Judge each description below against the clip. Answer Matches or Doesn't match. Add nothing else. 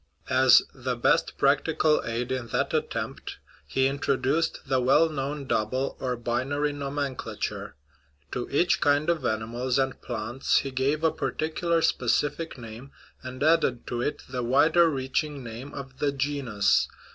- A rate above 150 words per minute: Doesn't match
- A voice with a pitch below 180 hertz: Matches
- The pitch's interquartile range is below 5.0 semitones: Matches